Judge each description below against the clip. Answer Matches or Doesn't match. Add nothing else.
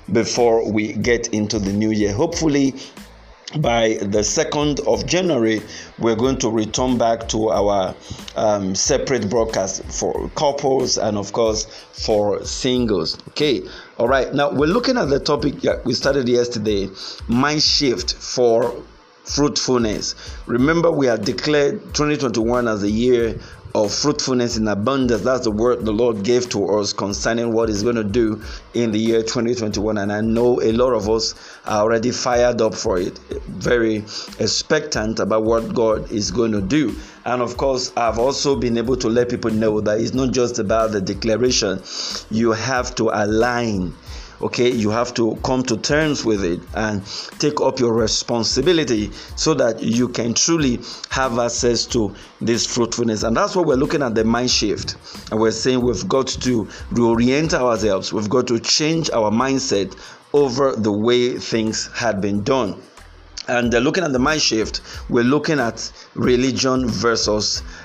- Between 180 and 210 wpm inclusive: Doesn't match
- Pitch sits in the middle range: Doesn't match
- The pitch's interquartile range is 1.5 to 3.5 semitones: Matches